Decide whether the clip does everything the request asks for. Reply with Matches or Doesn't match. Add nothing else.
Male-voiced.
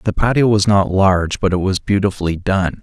Matches